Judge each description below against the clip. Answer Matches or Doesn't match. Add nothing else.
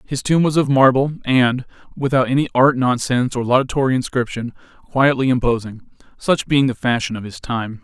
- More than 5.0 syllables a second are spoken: Matches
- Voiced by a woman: Doesn't match